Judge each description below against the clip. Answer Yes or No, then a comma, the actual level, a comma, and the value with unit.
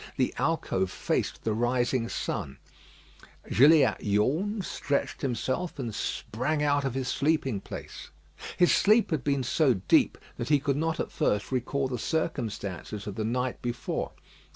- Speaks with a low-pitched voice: Yes, low, 130 Hz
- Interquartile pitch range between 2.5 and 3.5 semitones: No, average, 4.6 semitones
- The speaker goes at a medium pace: Yes, average, 150 wpm